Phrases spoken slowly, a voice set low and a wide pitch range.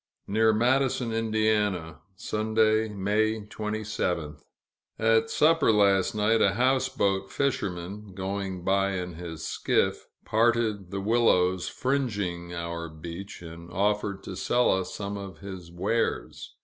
No: slow, 120 wpm; low, 100 Hz; average, 3.6 semitones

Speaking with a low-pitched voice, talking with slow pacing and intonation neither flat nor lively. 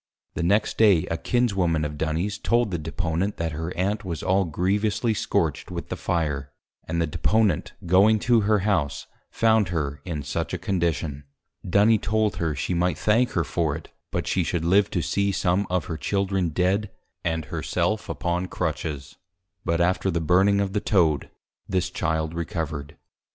No: very low, 90 Hz; average, 175 wpm; average, 3.8 semitones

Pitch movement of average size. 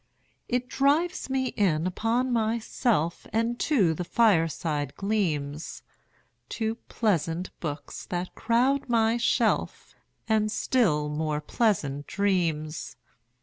No: wide, 6.8 semitones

